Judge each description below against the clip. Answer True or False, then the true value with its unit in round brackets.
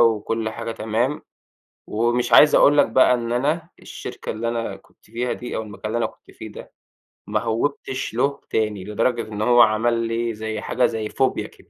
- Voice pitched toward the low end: True (115 Hz)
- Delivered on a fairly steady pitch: True (2.0 semitones)